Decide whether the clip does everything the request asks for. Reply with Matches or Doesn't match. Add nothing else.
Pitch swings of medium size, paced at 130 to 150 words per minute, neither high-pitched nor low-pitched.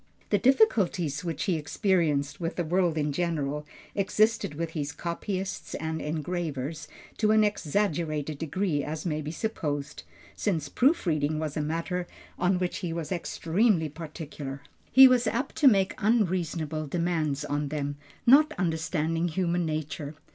Matches